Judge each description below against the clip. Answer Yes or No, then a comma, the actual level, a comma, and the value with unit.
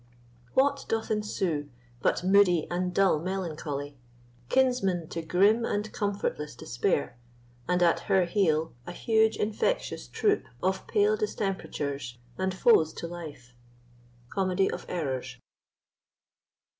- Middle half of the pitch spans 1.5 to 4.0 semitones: No, average, 5.2 semitones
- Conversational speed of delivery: No, slow, 115 wpm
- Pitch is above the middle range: No, medium, 180 Hz